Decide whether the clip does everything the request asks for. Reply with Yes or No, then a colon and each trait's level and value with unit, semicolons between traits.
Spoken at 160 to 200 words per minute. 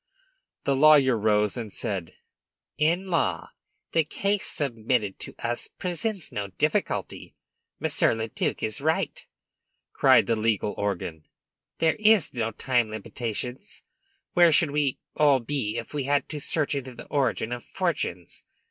No: average, 140 wpm